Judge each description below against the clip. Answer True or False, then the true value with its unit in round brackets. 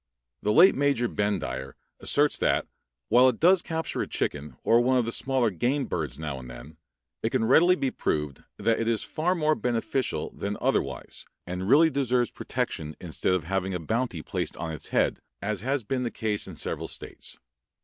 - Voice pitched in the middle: False (115 Hz)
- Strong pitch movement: True (7.1 semitones)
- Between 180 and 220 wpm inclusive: True (190 wpm)